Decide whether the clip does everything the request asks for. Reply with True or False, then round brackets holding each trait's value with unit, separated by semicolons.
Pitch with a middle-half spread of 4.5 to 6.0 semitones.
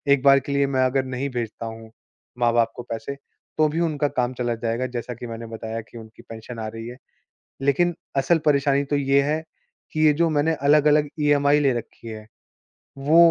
False (4.0 semitones)